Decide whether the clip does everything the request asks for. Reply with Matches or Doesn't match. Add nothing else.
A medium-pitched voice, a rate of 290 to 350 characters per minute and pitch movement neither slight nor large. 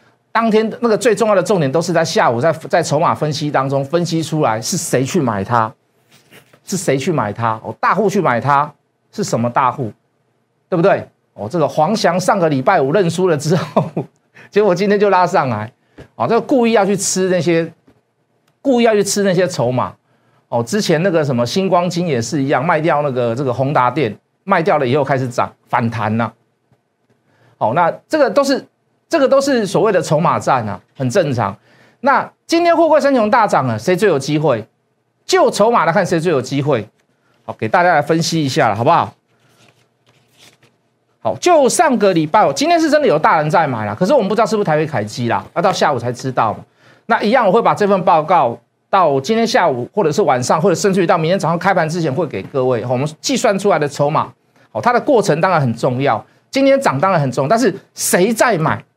Doesn't match